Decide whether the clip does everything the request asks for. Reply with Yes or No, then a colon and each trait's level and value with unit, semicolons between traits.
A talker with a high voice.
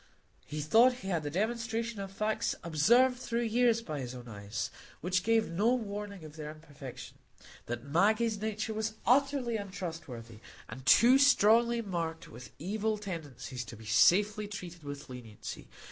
Yes: high, 195 Hz